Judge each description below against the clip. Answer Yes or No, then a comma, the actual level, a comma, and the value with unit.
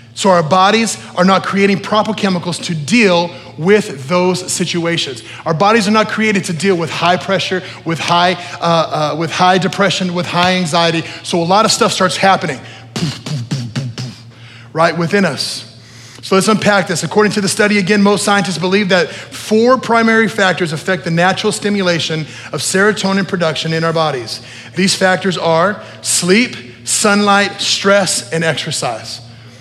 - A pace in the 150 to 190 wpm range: Yes, average, 170 wpm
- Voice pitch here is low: No, medium, 180 Hz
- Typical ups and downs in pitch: Yes, average, 4.1 semitones